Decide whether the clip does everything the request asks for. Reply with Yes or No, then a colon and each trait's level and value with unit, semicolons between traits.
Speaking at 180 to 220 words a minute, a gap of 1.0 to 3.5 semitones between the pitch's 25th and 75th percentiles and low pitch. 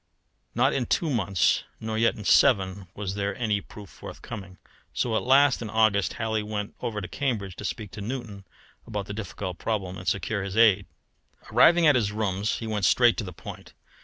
Yes: average, 190 wpm; average, 2.7 semitones; low, 105 Hz